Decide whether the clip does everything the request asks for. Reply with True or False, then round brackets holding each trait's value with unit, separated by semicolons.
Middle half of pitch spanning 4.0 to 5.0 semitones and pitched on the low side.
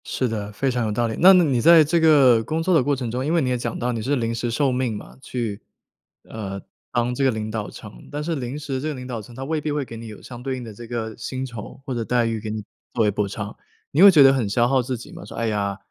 False (3.5 semitones; 125 Hz)